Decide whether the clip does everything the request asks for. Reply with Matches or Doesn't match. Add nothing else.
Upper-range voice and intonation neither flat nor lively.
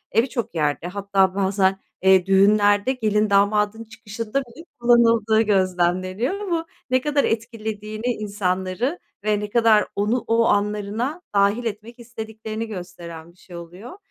Matches